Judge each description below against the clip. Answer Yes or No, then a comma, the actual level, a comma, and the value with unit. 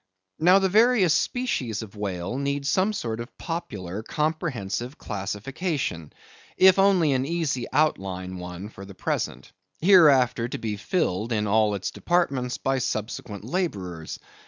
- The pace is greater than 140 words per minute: No, slow, 135 wpm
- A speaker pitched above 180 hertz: No, low, 125 Hz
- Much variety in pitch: Yes, wide, 8.5 semitones